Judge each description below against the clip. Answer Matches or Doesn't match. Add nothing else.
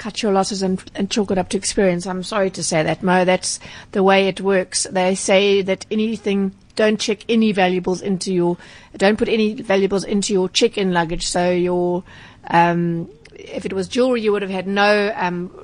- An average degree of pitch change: Doesn't match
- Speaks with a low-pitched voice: Doesn't match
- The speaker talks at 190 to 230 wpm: Matches